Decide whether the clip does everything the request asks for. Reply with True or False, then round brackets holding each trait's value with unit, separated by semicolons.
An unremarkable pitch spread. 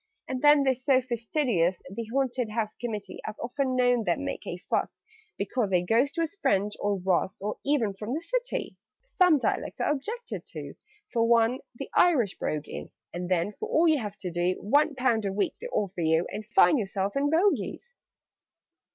False (6.0 semitones)